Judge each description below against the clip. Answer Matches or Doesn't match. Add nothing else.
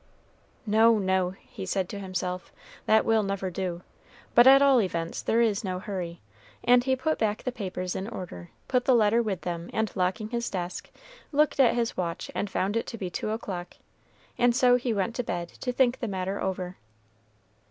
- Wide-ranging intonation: Doesn't match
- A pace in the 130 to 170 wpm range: Doesn't match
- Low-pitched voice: Doesn't match